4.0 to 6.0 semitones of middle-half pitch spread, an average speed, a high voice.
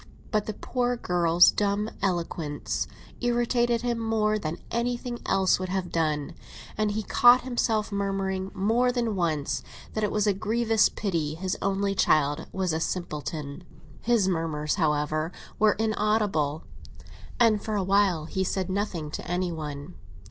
Yes: average, 4.8 semitones; average, 150 wpm; high, 195 Hz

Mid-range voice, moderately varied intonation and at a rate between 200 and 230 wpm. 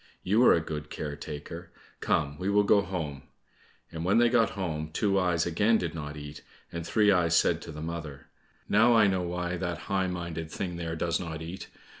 No: very low, 85 Hz; average, 3.2 semitones; fast, 205 wpm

